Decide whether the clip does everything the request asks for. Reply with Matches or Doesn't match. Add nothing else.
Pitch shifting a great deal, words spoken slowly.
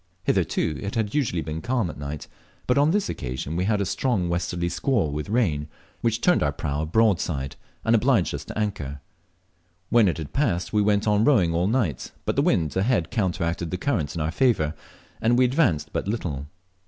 Doesn't match